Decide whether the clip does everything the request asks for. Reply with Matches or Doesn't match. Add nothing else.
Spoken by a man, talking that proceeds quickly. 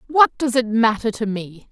Doesn't match